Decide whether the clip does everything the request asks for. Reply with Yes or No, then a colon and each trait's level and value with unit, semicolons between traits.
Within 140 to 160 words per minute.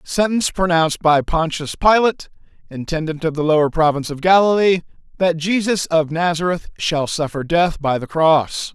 Yes: average, 150 wpm